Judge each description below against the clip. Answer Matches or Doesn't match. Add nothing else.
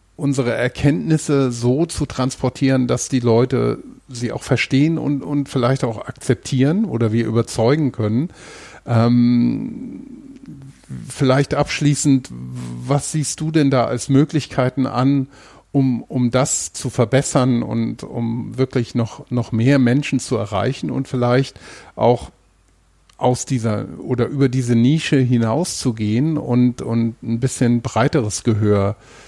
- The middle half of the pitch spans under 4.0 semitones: Matches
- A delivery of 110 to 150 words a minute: Matches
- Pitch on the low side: Matches